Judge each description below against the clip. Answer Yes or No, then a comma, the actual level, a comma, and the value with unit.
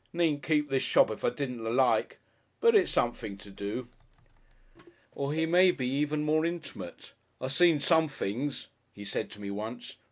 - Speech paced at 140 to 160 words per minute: No, average, 170 wpm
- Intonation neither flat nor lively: No, wide, 5.8 semitones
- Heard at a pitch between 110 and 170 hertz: Yes, medium, 140 Hz